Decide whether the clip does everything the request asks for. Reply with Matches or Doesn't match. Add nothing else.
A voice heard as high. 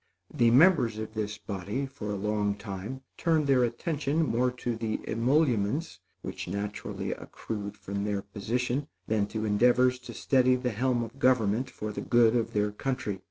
Doesn't match